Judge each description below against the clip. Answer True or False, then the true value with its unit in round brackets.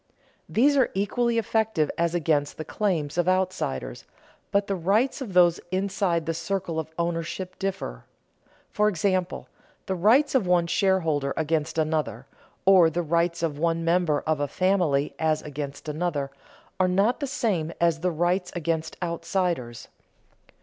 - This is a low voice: False (170 Hz)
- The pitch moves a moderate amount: True (3.3 semitones)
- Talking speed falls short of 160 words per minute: True (150 wpm)